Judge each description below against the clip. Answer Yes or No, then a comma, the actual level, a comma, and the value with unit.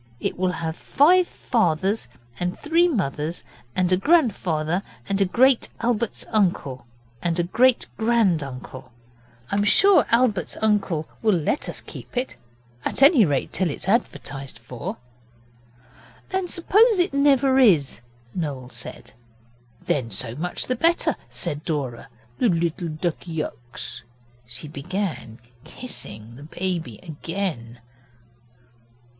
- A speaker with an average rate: No, slow, 125 wpm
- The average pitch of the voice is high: No, medium, 180 Hz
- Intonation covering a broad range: Yes, wide, 8.1 semitones